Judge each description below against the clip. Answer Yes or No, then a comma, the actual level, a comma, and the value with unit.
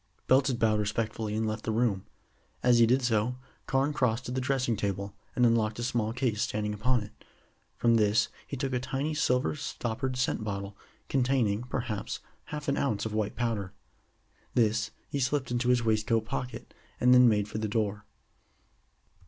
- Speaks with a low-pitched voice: Yes, low, 115 Hz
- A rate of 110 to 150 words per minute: No, average, 175 wpm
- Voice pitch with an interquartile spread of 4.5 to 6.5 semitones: No, average, 2.8 semitones